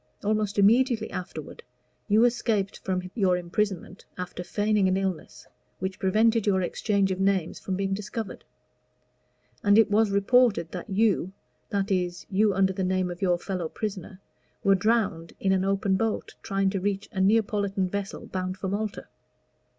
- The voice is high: Yes, high, 195 Hz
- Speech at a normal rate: Yes, average, 160 wpm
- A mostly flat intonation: Yes, narrow, 2.1 semitones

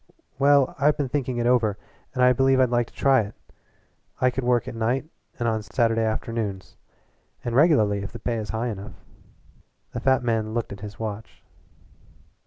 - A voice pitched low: Yes, low, 120 Hz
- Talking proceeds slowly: No, average, 185 wpm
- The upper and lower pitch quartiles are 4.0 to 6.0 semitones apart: No, average, 2.8 semitones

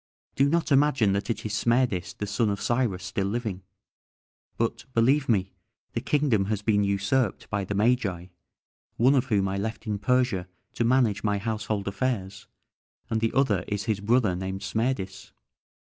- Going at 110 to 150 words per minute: No, average, 165 wpm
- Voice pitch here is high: No, low, 110 Hz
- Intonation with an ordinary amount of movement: Yes, average, 3.8 semitones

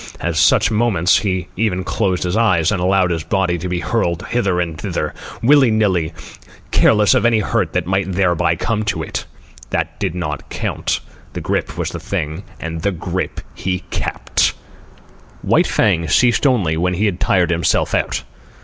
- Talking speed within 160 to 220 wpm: Yes, average, 175 wpm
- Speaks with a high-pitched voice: No, very low, 90 Hz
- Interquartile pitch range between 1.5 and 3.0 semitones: No, average, 3.7 semitones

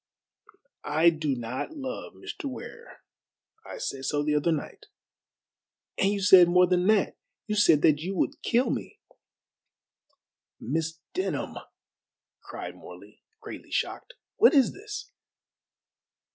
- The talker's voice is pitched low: No, medium, 185 Hz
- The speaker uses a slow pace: Yes, slow, 125 wpm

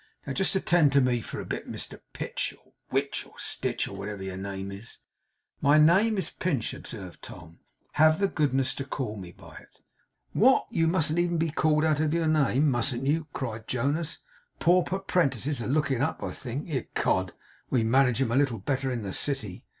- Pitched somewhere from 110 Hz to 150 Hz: Yes, medium, 140 Hz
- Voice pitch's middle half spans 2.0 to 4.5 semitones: No, average, 5.2 semitones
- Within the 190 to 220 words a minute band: Yes, average, 195 wpm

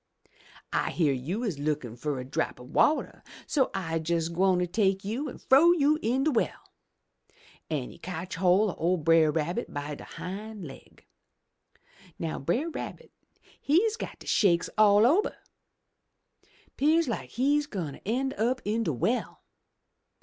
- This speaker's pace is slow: No, average, 155 wpm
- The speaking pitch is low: No, high, 195 Hz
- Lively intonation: Yes, wide, 7.9 semitones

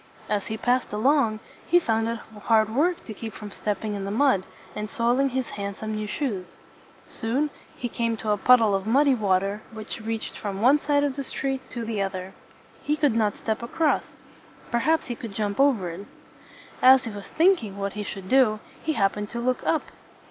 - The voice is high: Yes, high, 225 Hz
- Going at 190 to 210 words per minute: Yes, average, 200 wpm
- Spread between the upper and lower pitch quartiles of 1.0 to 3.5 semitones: No, average, 4.1 semitones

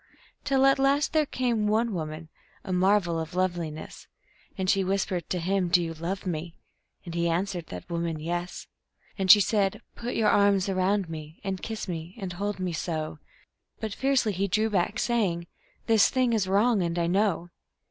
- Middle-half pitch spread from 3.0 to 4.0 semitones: Yes, average, 3.6 semitones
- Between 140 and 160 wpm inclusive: No, average, 185 wpm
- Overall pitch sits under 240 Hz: Yes, medium, 185 Hz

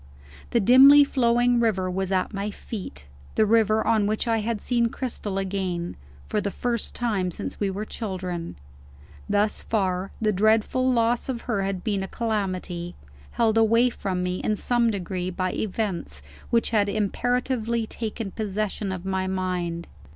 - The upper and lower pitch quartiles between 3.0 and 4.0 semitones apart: Yes, average, 3.5 semitones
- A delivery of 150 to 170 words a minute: Yes, average, 160 wpm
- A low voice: No, high, 210 Hz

